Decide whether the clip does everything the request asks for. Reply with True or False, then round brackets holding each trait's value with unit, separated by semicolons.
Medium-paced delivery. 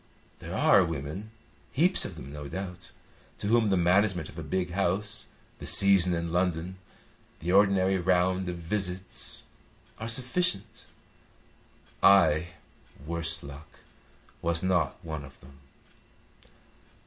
False (125 wpm)